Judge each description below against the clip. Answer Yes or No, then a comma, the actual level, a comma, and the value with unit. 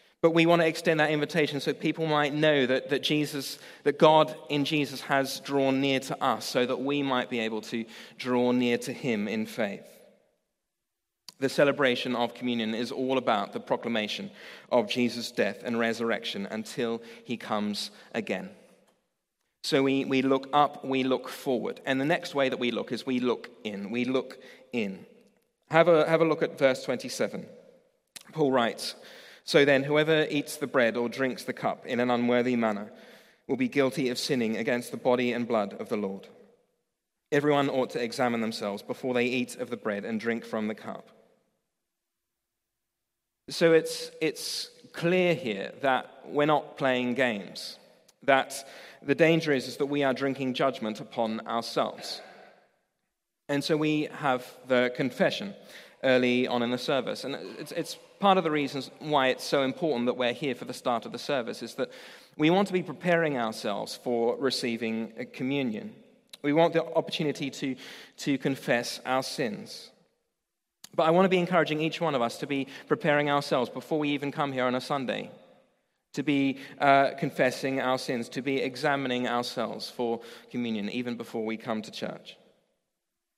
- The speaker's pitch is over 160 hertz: No, low, 135 Hz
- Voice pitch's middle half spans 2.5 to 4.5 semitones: Yes, average, 3.9 semitones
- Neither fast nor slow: Yes, average, 175 wpm